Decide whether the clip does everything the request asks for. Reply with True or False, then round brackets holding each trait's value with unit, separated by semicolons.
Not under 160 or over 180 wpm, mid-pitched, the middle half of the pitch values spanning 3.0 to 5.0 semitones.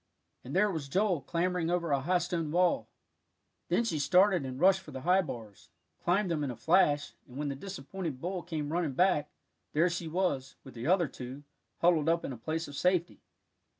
False (200 wpm; 165 Hz; 4.2 semitones)